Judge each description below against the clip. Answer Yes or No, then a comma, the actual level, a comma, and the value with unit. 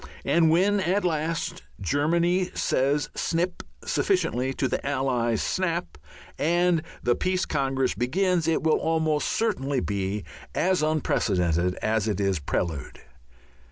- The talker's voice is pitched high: No, medium, 150 Hz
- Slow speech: Yes, slow, 120 wpm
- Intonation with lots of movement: Yes, wide, 6.4 semitones